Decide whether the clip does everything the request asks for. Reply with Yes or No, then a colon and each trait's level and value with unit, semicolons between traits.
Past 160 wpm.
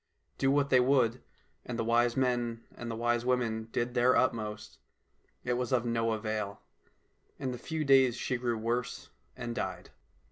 Yes: average, 180 wpm